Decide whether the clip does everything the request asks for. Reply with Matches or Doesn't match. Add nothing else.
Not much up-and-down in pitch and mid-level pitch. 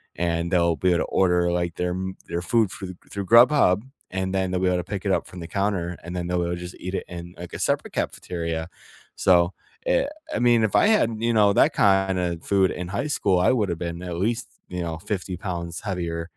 Doesn't match